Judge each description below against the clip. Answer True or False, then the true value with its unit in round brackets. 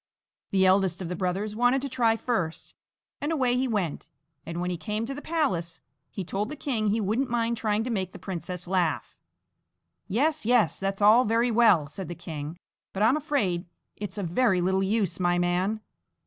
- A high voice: True (205 Hz)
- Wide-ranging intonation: False (4.7 semitones)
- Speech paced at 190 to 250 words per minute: True (195 wpm)